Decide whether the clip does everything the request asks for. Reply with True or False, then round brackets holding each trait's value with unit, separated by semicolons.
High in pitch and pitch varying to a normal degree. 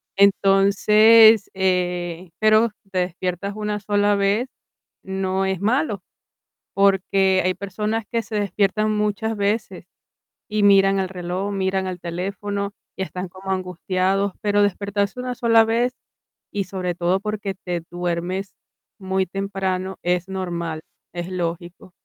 False (195 Hz; 1.9 semitones)